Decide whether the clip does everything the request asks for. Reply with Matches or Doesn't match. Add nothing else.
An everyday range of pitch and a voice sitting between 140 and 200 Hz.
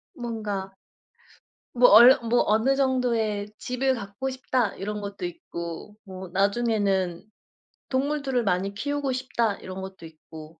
Doesn't match